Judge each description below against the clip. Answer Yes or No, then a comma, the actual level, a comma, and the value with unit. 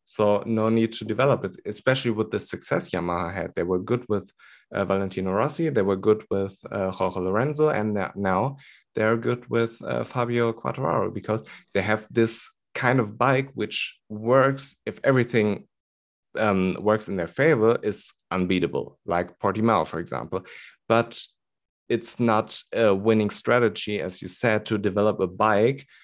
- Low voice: Yes, low, 110 Hz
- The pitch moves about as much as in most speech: Yes, average, 3.6 semitones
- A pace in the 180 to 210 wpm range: No, average, 160 wpm